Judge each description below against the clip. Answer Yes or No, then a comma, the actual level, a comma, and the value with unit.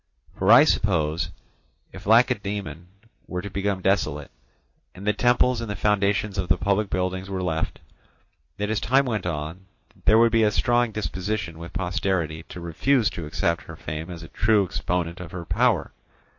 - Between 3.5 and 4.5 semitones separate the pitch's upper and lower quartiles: Yes, average, 3.8 semitones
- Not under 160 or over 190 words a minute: Yes, average, 170 wpm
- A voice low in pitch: Yes, very low, 95 Hz